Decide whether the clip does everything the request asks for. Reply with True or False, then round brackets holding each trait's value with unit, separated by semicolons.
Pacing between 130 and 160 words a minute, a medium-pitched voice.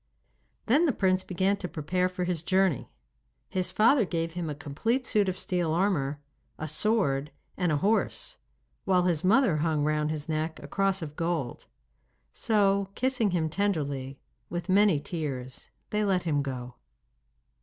True (155 wpm; 175 Hz)